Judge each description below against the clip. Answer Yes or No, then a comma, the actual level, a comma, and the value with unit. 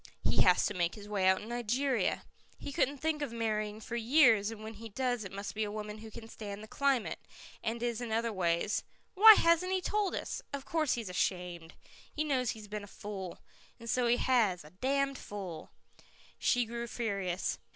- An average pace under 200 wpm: No, fast, 205 wpm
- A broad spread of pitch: No, average, 3.9 semitones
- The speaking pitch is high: Yes, high, 225 Hz